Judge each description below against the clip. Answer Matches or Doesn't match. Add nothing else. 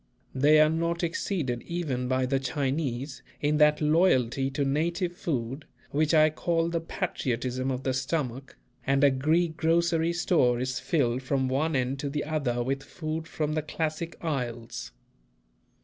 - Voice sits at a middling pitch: Matches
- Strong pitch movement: Doesn't match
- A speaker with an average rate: Matches